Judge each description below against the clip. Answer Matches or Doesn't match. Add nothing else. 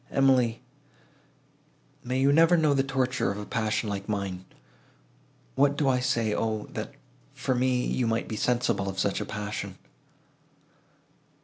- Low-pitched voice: Matches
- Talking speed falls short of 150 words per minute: Matches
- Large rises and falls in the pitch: Doesn't match